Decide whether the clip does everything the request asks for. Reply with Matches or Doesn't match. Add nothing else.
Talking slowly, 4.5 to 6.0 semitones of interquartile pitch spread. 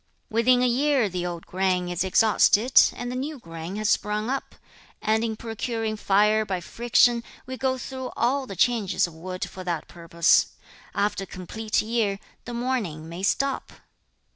Doesn't match